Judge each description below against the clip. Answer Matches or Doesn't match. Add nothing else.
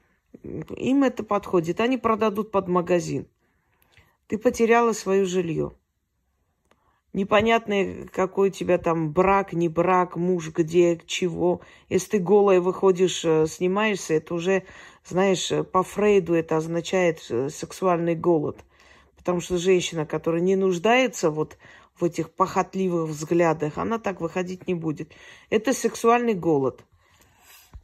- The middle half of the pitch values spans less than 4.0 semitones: Matches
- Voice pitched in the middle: Matches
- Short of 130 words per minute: Matches